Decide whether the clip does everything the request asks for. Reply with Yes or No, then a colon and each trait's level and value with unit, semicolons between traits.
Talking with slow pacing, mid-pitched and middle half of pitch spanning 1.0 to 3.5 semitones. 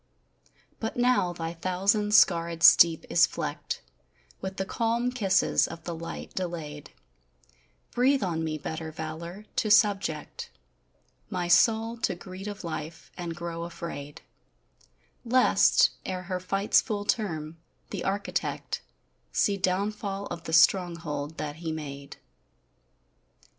No: slow, 120 wpm; medium, 180 Hz; average, 3.9 semitones